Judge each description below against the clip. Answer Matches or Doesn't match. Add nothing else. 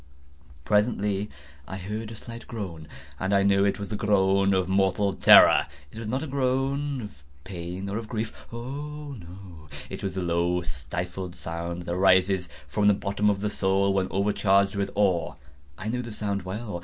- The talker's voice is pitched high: Doesn't match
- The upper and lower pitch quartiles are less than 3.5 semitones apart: Matches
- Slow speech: Doesn't match